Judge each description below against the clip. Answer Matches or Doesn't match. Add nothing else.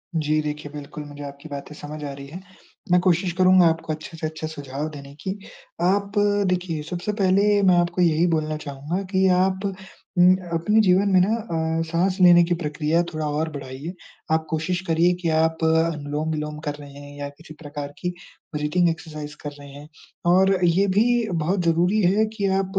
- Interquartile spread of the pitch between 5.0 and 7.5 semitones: Doesn't match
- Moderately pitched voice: Matches